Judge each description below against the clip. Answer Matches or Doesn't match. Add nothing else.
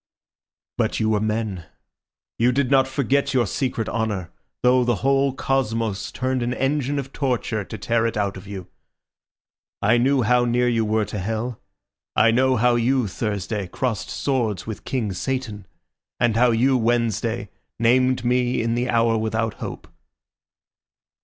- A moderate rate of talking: Matches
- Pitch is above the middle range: Doesn't match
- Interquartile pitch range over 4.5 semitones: Doesn't match